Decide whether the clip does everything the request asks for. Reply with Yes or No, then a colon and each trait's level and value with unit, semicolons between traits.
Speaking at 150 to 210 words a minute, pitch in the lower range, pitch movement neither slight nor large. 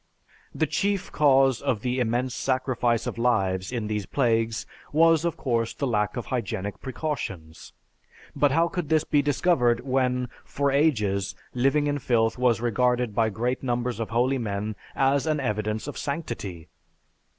Yes: average, 155 wpm; low, 125 Hz; average, 3.9 semitones